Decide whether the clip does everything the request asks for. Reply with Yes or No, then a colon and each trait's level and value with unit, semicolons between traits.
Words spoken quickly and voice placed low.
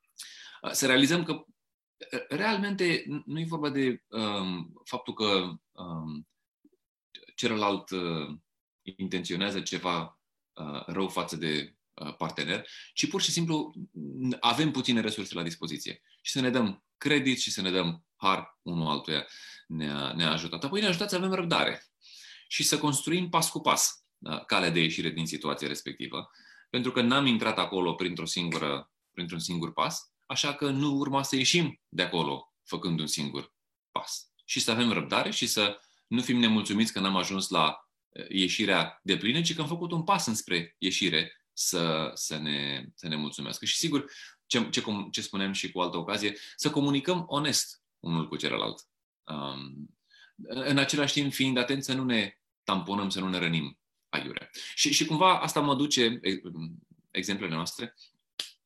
No: average, 155 wpm; low, 100 Hz